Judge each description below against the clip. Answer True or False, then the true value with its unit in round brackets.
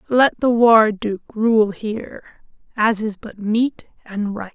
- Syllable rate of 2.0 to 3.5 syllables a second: True (3.4 syllables/s)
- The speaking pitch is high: True (220 Hz)